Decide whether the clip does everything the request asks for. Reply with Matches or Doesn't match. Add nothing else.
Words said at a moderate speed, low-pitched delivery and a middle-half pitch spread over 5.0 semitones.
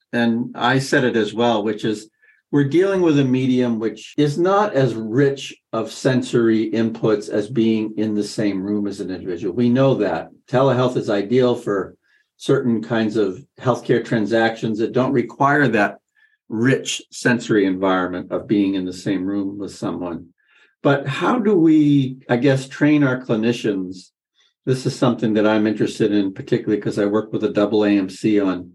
Doesn't match